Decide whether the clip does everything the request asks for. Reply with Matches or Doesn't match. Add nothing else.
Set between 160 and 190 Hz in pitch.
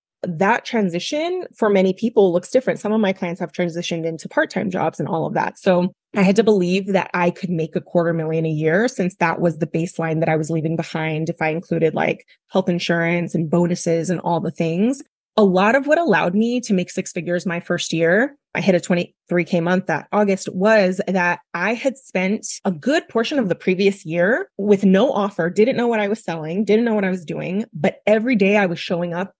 Matches